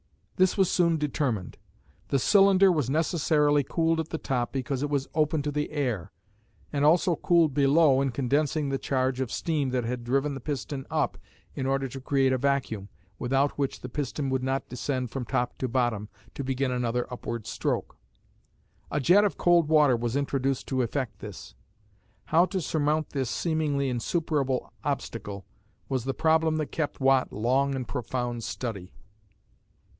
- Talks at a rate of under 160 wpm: No, average, 170 wpm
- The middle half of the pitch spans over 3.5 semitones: No, average, 3.2 semitones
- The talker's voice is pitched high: No, low, 135 Hz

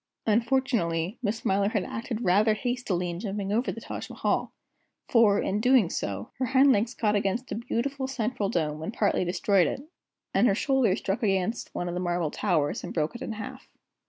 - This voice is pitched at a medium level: No, high, 210 Hz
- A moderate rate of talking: Yes, average, 190 wpm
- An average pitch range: Yes, average, 4.8 semitones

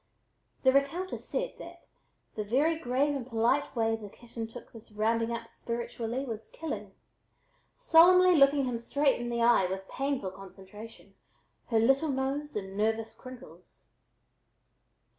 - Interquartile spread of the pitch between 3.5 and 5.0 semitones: Yes, average, 4.0 semitones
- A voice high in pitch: Yes, high, 240 Hz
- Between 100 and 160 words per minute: Yes, average, 140 wpm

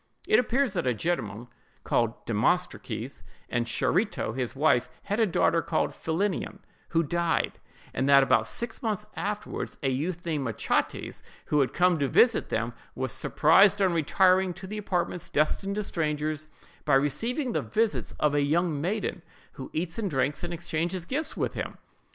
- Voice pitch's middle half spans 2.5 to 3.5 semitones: No, wide, 5.4 semitones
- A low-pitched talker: No, medium, 170 Hz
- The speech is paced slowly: No, average, 165 wpm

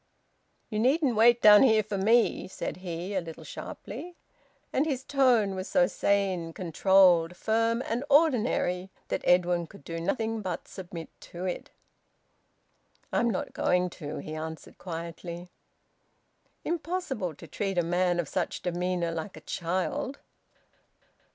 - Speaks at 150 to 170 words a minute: No, average, 140 wpm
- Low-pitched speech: No, high, 190 Hz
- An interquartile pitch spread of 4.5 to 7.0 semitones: Yes, average, 4.9 semitones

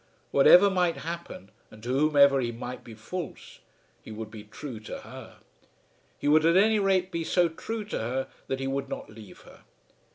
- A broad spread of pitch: Yes, wide, 7.0 semitones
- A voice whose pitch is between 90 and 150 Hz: Yes, medium, 140 Hz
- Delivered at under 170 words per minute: No, average, 190 wpm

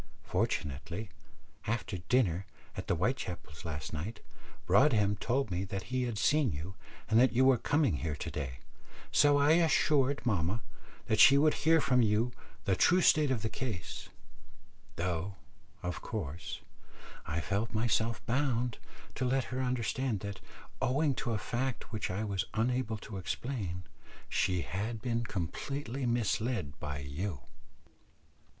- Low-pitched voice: Yes, low, 110 Hz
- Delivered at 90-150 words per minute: Yes, average, 145 wpm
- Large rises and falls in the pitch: Yes, wide, 5.8 semitones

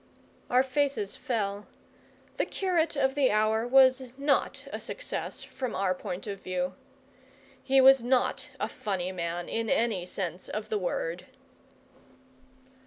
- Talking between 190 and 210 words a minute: No, slow, 135 wpm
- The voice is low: No, high, 220 Hz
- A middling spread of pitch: No, wide, 6.0 semitones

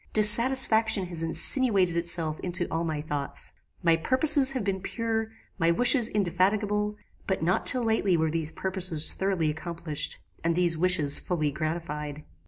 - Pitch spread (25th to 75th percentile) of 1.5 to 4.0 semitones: No, average, 4.5 semitones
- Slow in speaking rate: No, average, 145 wpm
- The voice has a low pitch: No, medium, 180 Hz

